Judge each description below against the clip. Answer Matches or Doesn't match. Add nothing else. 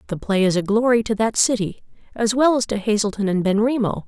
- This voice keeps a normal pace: Doesn't match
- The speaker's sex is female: Matches